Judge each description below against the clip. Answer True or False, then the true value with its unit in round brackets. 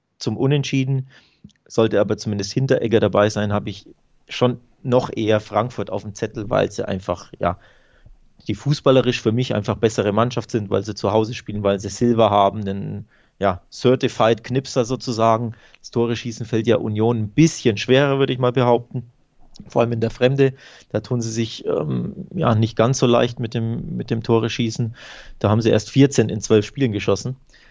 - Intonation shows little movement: False (3.0 semitones)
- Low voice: True (115 Hz)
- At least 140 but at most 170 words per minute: False (185 wpm)